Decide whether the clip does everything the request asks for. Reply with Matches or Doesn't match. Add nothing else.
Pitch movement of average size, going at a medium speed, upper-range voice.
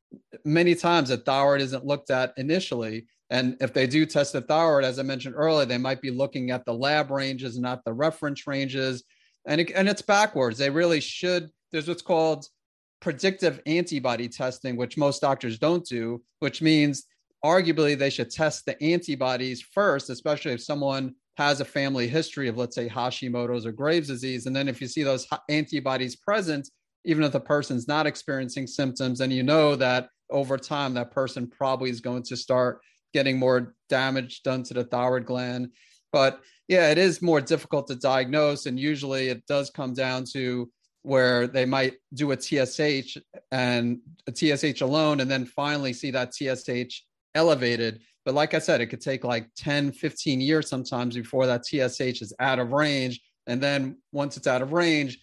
Doesn't match